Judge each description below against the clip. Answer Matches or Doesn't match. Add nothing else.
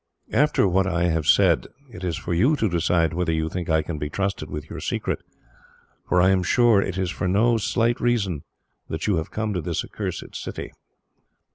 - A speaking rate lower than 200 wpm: Doesn't match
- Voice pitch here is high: Doesn't match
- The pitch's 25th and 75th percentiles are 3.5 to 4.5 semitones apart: Matches